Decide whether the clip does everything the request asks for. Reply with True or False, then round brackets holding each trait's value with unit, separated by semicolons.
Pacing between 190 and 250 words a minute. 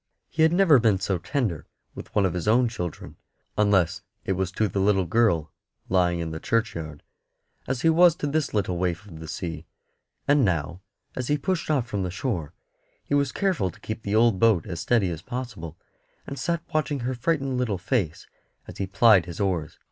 True (200 wpm)